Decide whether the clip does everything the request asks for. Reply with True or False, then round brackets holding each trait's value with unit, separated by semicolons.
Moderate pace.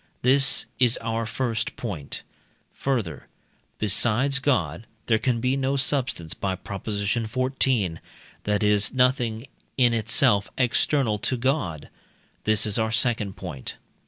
False (125 wpm)